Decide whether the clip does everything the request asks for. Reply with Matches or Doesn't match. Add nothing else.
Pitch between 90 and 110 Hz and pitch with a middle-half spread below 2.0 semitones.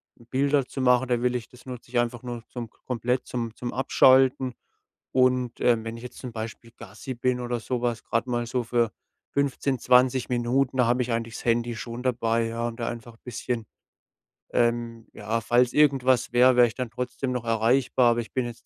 Doesn't match